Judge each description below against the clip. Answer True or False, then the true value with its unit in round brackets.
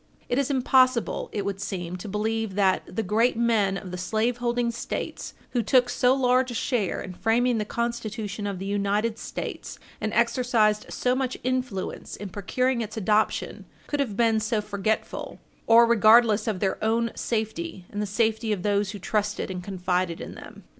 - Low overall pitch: False (220 Hz)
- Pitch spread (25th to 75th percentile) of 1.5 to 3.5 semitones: True (2.9 semitones)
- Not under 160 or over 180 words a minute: True (175 wpm)